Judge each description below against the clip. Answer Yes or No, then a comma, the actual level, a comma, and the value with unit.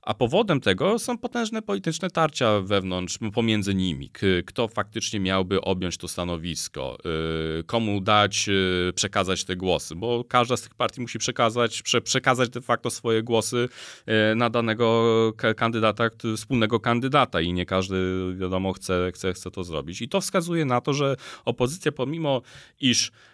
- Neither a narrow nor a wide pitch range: Yes, average, 4.7 semitones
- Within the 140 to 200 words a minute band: Yes, average, 145 wpm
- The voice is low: Yes, low, 115 Hz